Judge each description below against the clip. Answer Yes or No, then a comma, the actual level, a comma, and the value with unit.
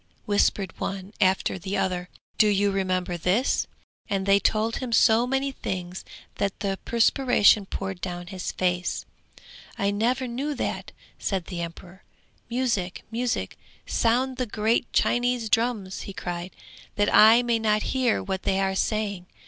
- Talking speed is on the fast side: No, average, 150 wpm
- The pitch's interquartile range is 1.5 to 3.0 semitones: No, average, 3.8 semitones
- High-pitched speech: Yes, high, 205 Hz